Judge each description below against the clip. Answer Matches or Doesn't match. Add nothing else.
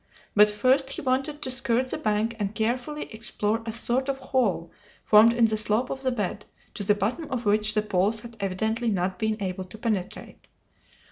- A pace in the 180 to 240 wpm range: Matches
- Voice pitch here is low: Doesn't match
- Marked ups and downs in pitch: Doesn't match